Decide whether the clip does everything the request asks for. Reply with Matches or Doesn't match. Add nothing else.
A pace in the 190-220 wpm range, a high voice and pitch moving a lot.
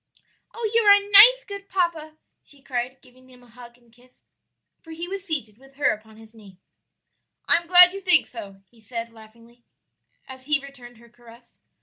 Matches